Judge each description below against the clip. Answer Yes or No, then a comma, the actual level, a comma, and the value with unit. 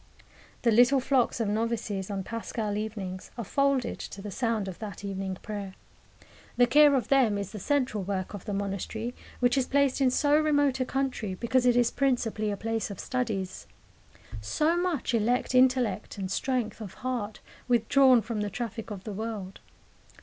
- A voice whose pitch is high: Yes, high, 230 Hz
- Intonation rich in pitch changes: No, average, 4.0 semitones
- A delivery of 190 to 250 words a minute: No, average, 175 wpm